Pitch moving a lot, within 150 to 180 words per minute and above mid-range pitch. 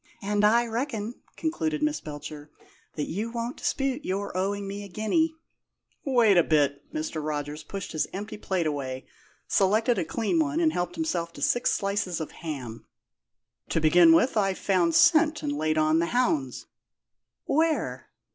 Yes: wide, 7.3 semitones; average, 160 wpm; high, 195 Hz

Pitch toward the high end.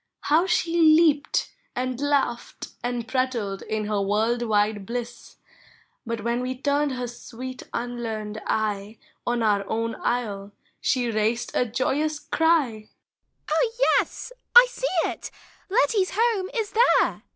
Yes: high, 245 Hz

